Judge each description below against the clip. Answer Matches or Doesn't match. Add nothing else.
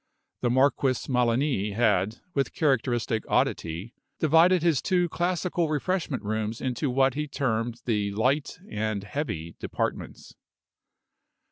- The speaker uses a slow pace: Matches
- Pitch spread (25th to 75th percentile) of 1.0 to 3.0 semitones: Doesn't match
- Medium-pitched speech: Doesn't match